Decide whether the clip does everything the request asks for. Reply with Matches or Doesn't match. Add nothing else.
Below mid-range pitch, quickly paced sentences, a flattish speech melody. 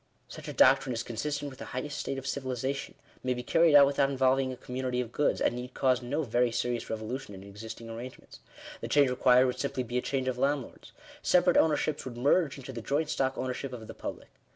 Matches